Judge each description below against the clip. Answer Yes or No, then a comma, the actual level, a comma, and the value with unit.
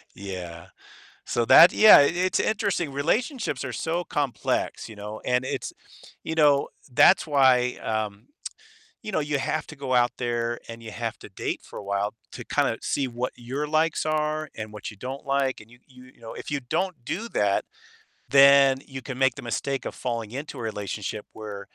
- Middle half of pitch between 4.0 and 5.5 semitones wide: Yes, average, 4.6 semitones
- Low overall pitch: Yes, low, 130 Hz